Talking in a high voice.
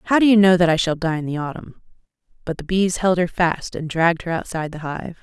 No: medium, 170 Hz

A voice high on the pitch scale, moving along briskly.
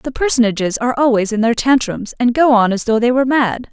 Yes: high, 240 Hz; fast, 240 wpm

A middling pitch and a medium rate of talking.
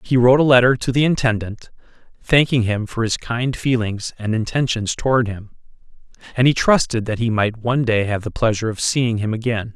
No: low, 115 Hz; average, 195 wpm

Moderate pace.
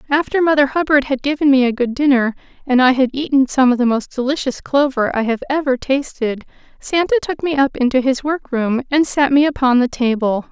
No: fast, 210 wpm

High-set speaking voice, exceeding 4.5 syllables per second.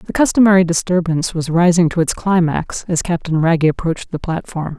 No: medium, 170 Hz; 5.7 syllables/s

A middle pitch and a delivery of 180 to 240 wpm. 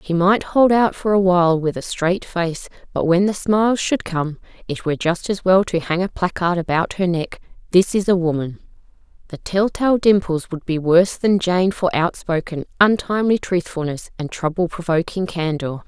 Yes: medium, 180 Hz; average, 185 wpm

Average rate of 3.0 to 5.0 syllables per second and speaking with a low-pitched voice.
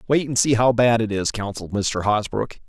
No: 5.2 syllables/s; low, 115 Hz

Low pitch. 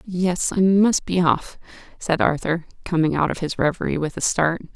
No: medium, 170 Hz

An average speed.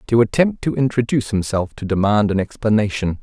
Yes: average, 165 wpm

